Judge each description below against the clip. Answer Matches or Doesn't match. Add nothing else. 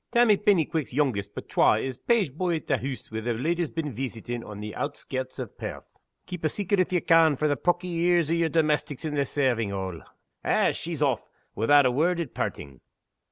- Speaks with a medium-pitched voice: Matches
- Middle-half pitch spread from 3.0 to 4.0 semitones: Doesn't match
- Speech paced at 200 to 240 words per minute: Matches